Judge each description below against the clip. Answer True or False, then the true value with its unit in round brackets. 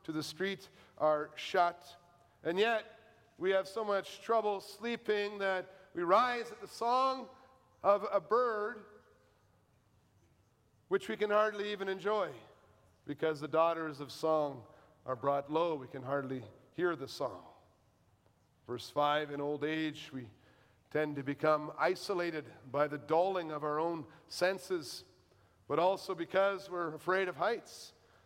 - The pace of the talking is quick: False (140 wpm)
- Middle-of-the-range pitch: True (165 Hz)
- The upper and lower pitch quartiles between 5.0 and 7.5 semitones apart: True (5.5 semitones)